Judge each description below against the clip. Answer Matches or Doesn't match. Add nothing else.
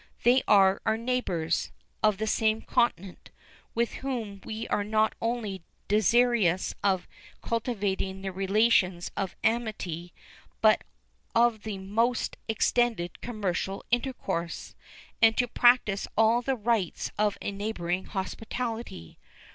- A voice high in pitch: Matches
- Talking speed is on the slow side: Matches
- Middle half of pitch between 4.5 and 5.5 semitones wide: Doesn't match